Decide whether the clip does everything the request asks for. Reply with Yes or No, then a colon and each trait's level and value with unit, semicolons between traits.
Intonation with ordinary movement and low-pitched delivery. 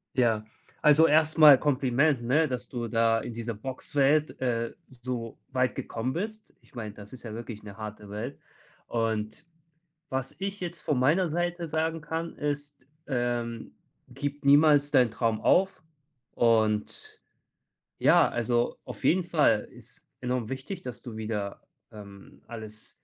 Yes: average, 4.7 semitones; low, 125 Hz